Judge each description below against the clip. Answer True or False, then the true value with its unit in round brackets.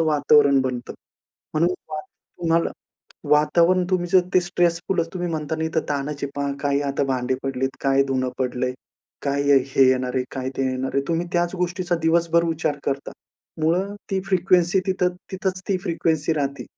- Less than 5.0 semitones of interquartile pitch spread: True (4.1 semitones)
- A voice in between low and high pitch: True (155 Hz)